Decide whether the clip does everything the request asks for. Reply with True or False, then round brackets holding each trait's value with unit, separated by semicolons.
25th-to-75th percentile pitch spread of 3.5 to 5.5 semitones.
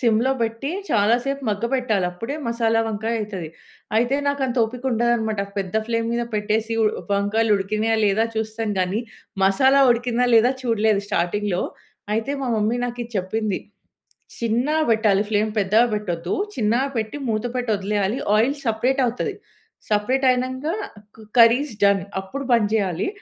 False (2.6 semitones)